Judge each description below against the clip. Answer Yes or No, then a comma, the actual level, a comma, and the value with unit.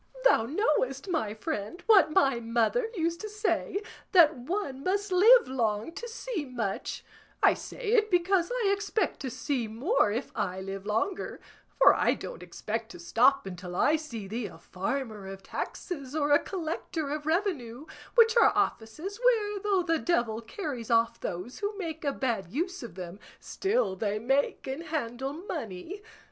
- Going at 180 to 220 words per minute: No, average, 165 wpm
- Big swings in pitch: Yes, wide, 9.0 semitones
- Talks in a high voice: Yes, very high, 290 Hz